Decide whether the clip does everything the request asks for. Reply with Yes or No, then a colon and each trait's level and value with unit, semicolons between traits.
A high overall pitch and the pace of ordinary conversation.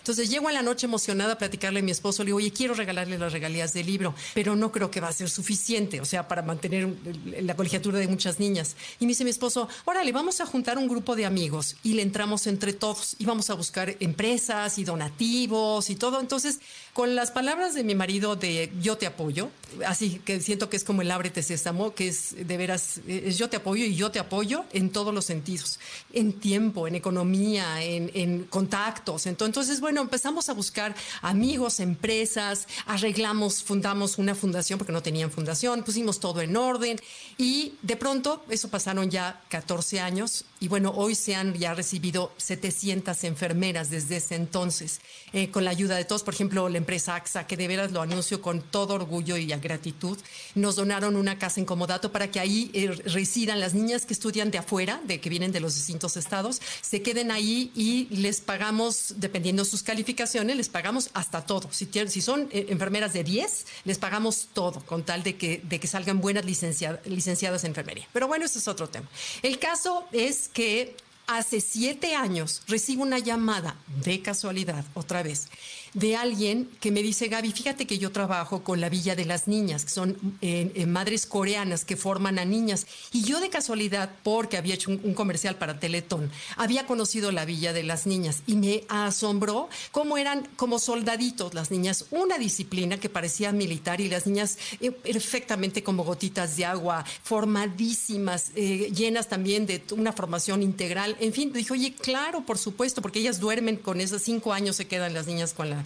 No: high, 200 Hz; fast, 195 wpm